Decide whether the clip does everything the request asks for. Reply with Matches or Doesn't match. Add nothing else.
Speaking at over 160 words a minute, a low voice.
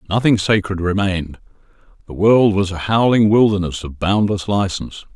Doesn't match